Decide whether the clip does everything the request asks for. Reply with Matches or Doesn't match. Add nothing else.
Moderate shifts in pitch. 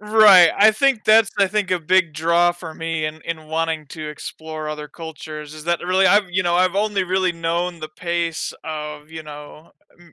Matches